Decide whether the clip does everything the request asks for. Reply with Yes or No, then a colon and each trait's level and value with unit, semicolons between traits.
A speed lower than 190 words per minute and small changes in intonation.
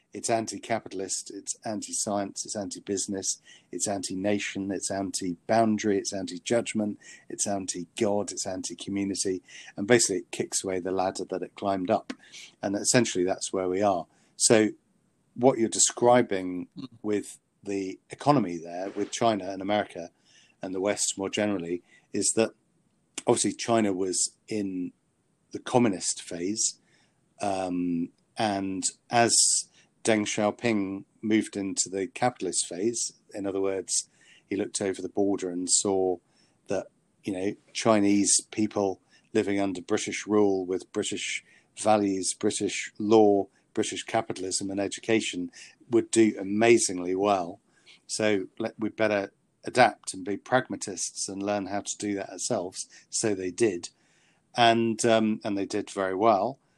Yes: average, 140 wpm; narrow, 2.3 semitones